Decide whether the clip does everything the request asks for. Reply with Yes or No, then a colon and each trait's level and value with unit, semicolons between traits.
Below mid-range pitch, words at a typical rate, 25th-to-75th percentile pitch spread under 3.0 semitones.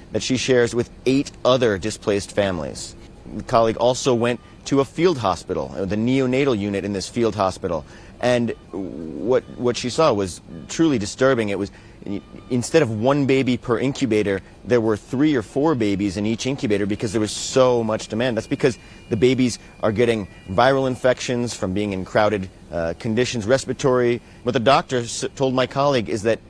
No: low, 115 Hz; average, 175 wpm; average, 3.9 semitones